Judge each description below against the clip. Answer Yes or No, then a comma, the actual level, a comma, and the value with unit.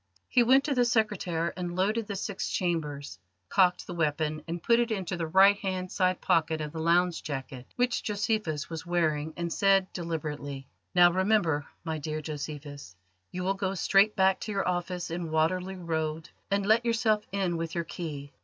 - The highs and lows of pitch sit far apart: No, average, 3.7 semitones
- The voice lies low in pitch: No, medium, 175 Hz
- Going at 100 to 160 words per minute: No, average, 180 wpm